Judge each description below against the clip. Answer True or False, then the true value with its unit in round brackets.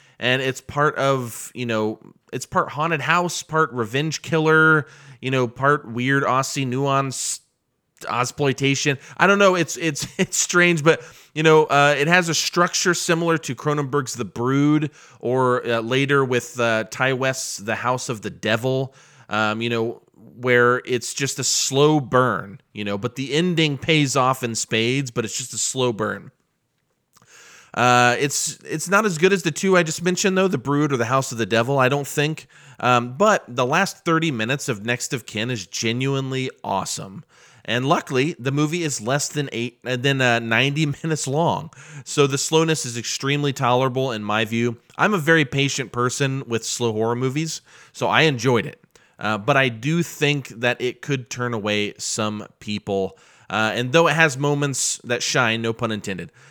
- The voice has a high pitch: False (135 Hz)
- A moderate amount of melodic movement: True (3.9 semitones)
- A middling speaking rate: True (185 wpm)